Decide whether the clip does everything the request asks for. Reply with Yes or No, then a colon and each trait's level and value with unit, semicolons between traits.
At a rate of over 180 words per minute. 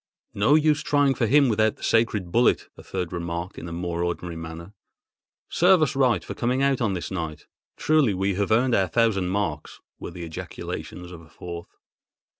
Yes: average, 190 wpm